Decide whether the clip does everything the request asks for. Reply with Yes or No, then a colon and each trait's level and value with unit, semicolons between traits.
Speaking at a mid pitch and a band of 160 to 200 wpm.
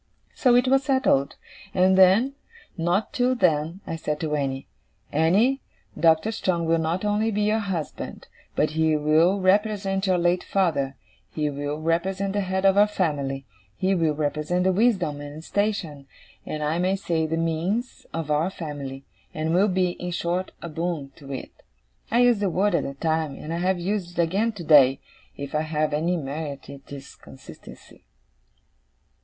Yes: medium, 170 Hz; average, 175 wpm